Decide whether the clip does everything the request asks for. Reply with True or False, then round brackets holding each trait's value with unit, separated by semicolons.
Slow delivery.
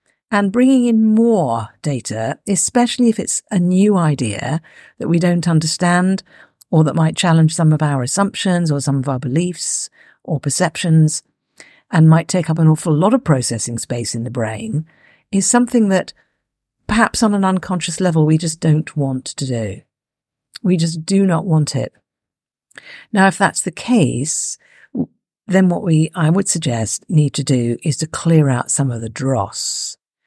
False (170 wpm)